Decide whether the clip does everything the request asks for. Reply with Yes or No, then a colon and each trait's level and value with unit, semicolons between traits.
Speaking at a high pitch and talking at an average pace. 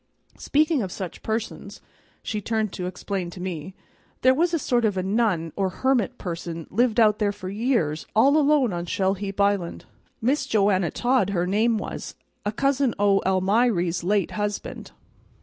Yes: high, 205 Hz; average, 165 wpm